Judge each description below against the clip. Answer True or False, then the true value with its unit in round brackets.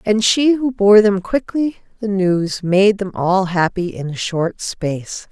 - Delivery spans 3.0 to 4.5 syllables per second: True (3.8 syllables/s)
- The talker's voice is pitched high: True (200 Hz)